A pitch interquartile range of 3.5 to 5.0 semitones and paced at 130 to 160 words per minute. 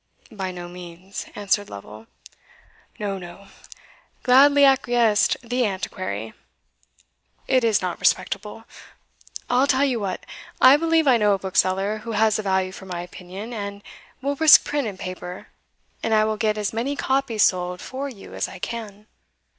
Yes: average, 4.6 semitones; average, 155 wpm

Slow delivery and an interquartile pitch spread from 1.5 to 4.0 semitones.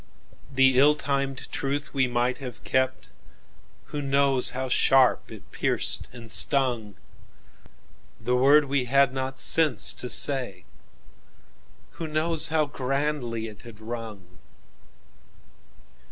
Yes: slow, 105 wpm; average, 2.7 semitones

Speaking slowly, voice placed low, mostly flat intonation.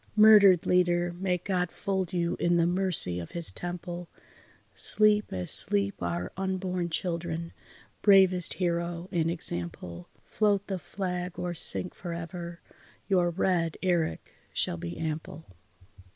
No: slow, 130 wpm; medium, 175 Hz; narrow, 2.0 semitones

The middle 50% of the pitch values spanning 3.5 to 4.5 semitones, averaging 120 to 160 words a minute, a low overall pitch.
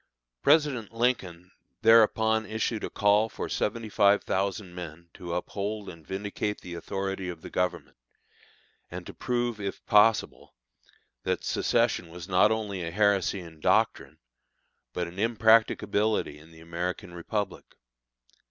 Yes: average, 3.8 semitones; slow, 135 wpm; low, 100 Hz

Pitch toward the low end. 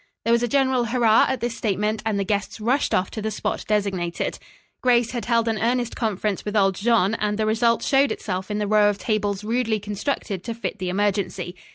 No: high, 215 Hz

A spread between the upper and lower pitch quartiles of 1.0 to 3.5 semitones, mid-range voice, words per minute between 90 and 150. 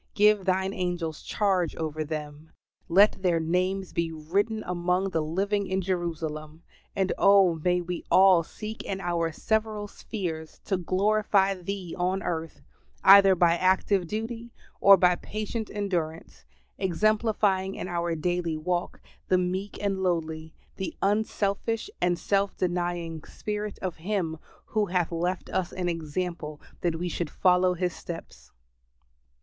Yes: average, 2.8 semitones; medium, 180 Hz; average, 140 wpm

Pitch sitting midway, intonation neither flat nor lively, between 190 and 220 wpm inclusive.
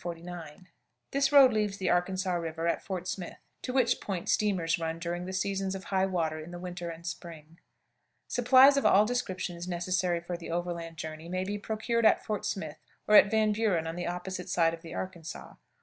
Yes: medium, 180 Hz; average, 3.3 semitones; average, 195 wpm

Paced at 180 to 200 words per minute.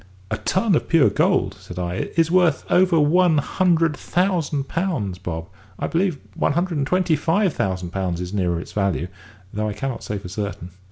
Yes: average, 185 wpm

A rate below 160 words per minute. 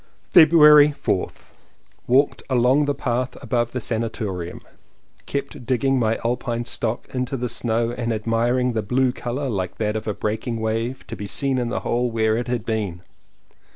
No: average, 170 wpm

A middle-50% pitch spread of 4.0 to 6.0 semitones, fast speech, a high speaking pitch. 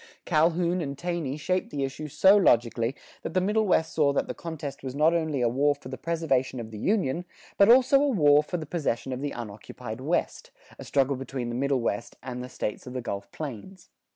No: average, 5.3 semitones; fast, 215 wpm; medium, 145 Hz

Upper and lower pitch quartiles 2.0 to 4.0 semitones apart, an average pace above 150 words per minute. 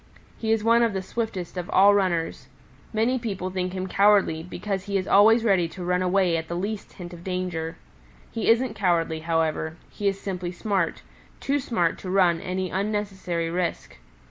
Yes: average, 3.0 semitones; average, 180 wpm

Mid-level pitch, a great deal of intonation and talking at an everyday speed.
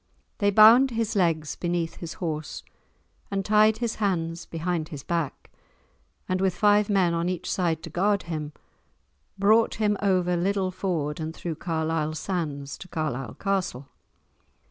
No: medium, 175 Hz; average, 3.8 semitones; average, 145 wpm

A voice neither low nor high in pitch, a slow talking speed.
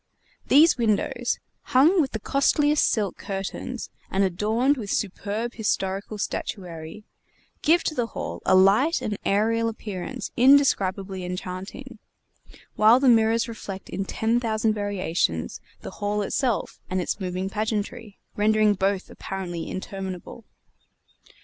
No: high, 210 Hz; slow, 125 wpm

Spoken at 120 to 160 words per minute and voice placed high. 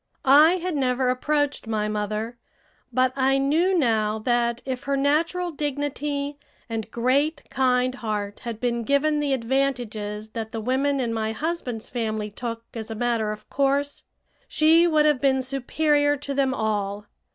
Yes: average, 155 wpm; very high, 260 Hz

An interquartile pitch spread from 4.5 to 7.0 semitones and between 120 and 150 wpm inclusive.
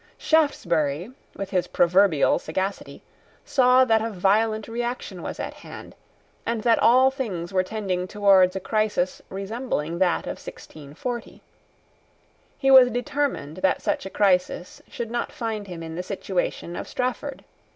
Yes: average, 4.8 semitones; average, 140 wpm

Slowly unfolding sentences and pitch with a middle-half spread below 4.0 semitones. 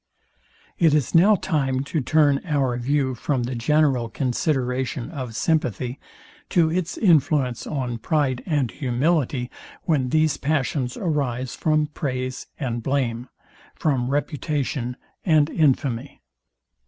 Yes: slow, 115 wpm; average, 3.5 semitones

